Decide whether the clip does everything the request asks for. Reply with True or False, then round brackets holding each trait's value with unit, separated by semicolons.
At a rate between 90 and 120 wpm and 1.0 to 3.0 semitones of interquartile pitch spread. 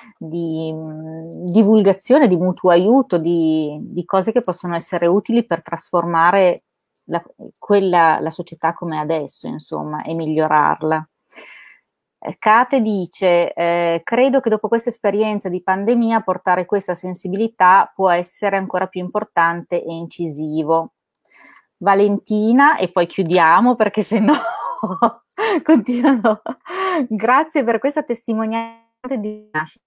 False (115 wpm; 5.1 semitones)